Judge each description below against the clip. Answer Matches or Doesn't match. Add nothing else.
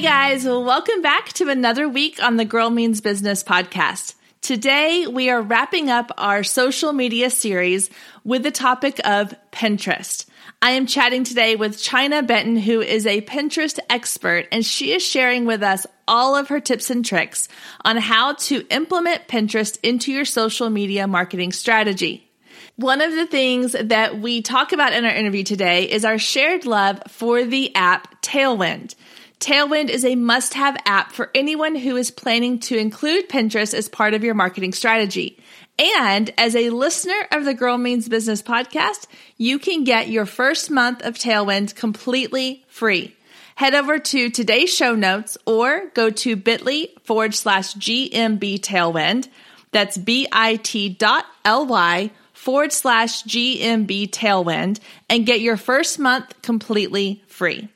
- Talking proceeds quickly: Doesn't match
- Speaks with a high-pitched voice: Matches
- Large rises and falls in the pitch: Doesn't match